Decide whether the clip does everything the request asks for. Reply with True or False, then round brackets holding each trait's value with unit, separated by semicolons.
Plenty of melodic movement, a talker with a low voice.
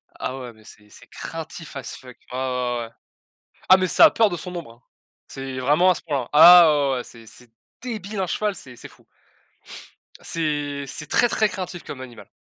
False (6.1 semitones; 145 Hz)